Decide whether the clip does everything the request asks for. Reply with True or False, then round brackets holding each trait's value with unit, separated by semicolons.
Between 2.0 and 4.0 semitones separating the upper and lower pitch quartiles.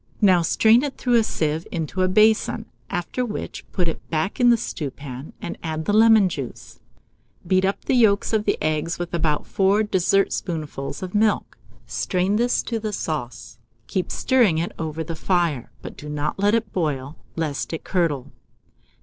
False (5.2 semitones)